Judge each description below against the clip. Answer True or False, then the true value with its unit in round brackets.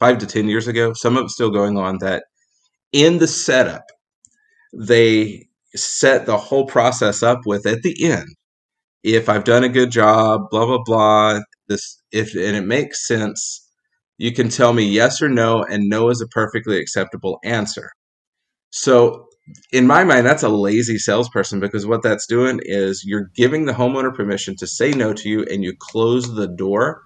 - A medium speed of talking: True (180 wpm)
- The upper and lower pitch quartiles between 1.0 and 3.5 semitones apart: True (2.8 semitones)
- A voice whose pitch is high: False (115 Hz)